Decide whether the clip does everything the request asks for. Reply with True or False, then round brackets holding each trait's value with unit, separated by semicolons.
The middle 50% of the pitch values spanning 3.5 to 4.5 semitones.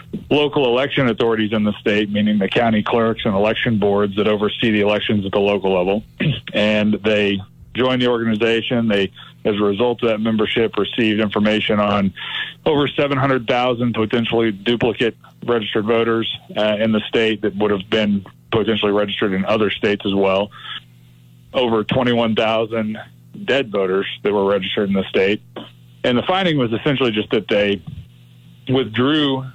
False (2.5 semitones)